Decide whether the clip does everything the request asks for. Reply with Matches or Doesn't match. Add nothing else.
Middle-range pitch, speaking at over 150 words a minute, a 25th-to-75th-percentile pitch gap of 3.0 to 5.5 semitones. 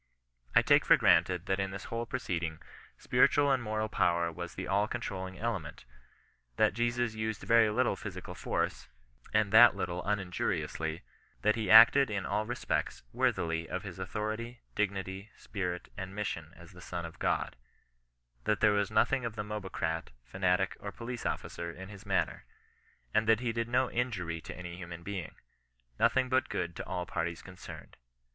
Doesn't match